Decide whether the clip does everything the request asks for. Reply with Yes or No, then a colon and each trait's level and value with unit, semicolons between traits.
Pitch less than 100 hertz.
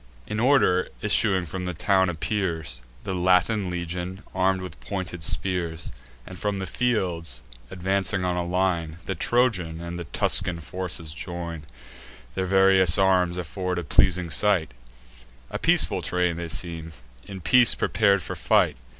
Yes: very low, 90 Hz